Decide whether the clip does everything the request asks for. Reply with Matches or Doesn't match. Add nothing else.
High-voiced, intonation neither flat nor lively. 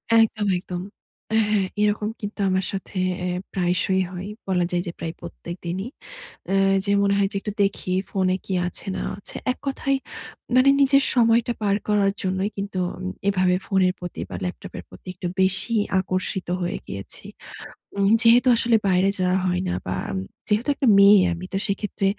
Doesn't match